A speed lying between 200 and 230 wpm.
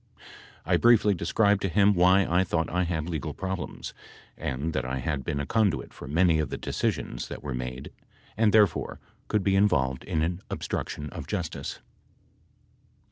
No: average, 170 wpm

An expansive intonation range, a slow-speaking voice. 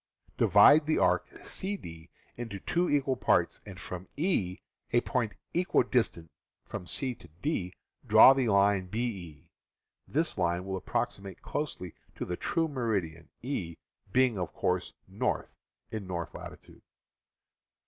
Yes: wide, 6.8 semitones; slow, 130 wpm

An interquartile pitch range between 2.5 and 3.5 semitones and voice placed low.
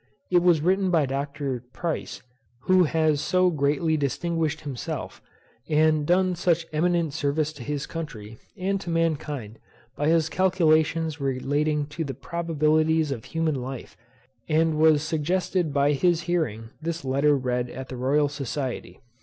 No: average, 2.9 semitones; medium, 155 Hz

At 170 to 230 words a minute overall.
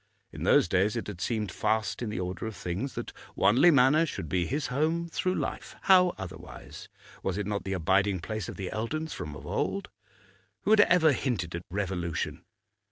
Yes: average, 190 wpm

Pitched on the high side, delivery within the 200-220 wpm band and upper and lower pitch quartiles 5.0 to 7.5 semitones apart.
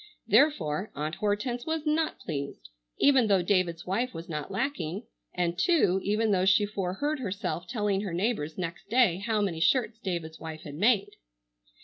No: high, 195 Hz; average, 160 wpm; average, 5.3 semitones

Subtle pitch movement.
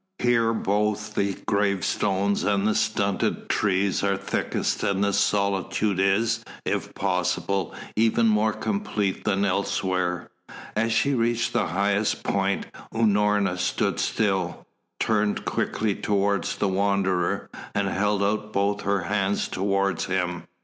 Yes: narrow, 1.4 semitones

